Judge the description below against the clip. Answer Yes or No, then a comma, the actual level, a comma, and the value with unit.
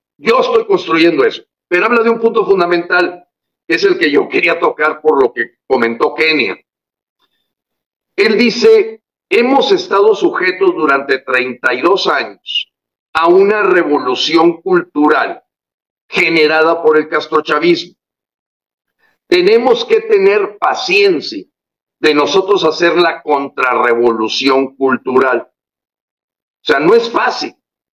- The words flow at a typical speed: No, slow, 115 wpm